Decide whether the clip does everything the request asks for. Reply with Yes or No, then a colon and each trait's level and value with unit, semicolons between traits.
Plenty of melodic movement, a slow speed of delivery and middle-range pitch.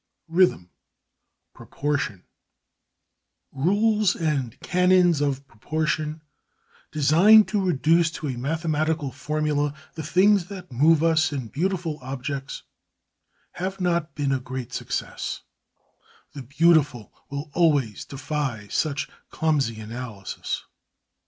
No: average, 4.0 semitones; slow, 105 wpm; medium, 150 Hz